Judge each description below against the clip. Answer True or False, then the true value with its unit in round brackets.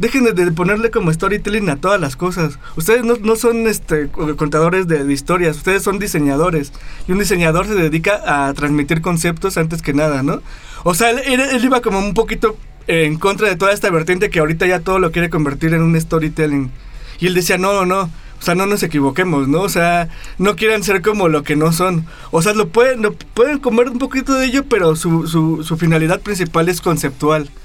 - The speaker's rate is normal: False (210 wpm)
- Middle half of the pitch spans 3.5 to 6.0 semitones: True (4.5 semitones)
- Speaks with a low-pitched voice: False (180 Hz)